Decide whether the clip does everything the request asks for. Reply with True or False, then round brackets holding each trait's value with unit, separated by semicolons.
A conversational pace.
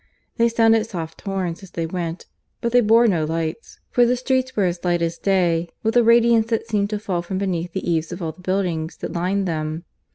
False (225 wpm)